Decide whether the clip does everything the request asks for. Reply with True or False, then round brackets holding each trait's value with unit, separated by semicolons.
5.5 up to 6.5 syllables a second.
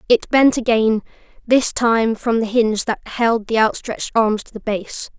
False (4.5 syllables/s)